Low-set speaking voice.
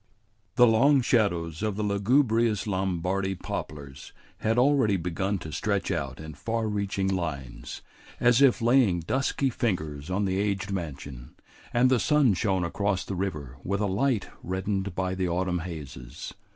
Yes: very low, 95 Hz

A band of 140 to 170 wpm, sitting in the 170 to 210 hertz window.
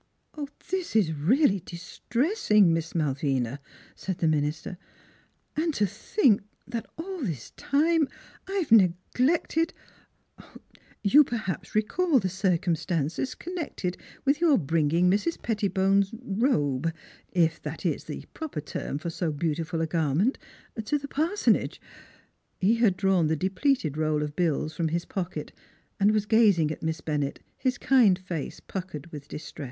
Yes: average, 145 wpm; high, 190 Hz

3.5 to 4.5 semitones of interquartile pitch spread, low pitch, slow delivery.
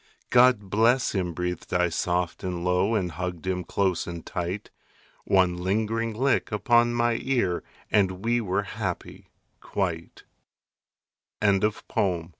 Yes: average, 3.9 semitones; very low, 95 Hz; slow, 125 wpm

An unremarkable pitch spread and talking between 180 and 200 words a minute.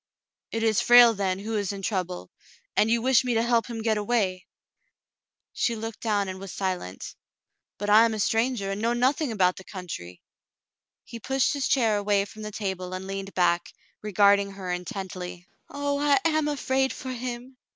Yes: average, 3.9 semitones; average, 190 wpm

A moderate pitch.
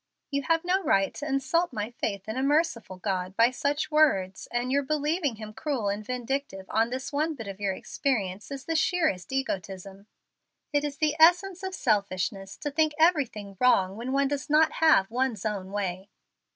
No: very high, 255 Hz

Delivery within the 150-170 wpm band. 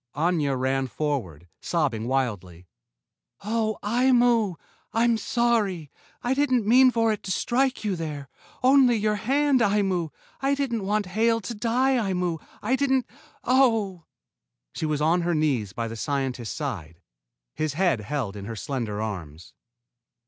No: average, 140 wpm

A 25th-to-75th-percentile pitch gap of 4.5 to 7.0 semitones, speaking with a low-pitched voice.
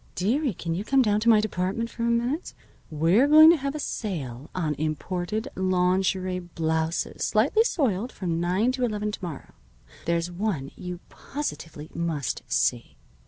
No: wide, 5.6 semitones; high, 190 Hz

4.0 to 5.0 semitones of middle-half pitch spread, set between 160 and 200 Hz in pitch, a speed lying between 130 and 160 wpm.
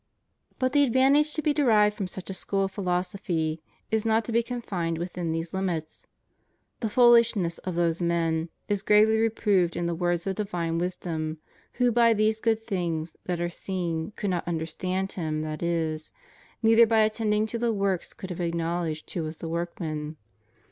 No: average, 4.7 semitones; medium, 185 Hz; average, 175 wpm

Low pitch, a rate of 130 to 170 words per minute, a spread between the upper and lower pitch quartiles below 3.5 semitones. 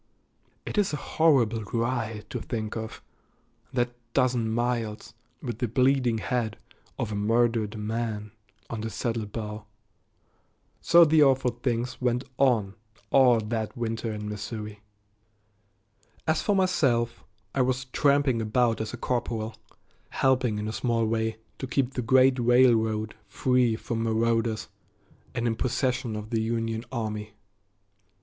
Yes: low, 115 Hz; slow, 135 wpm; narrow, 2.4 semitones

